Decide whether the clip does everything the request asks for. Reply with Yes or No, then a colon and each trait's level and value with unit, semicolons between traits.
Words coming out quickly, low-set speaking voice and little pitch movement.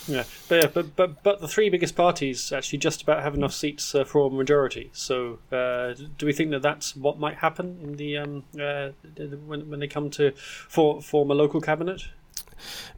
No: fast, 215 wpm; medium, 145 Hz; narrow, 2.0 semitones